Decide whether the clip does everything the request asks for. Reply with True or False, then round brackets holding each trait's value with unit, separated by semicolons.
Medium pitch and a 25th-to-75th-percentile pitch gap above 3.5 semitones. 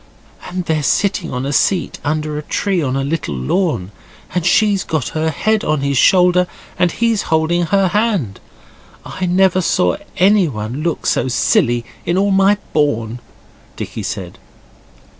True (165 Hz; 5.4 semitones)